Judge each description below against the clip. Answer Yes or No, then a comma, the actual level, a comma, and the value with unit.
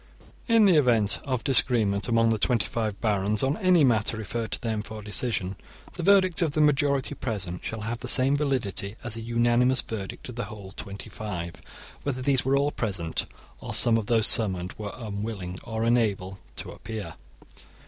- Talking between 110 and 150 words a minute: No, average, 185 wpm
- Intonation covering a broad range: No, average, 4.0 semitones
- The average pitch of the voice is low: Yes, low, 115 Hz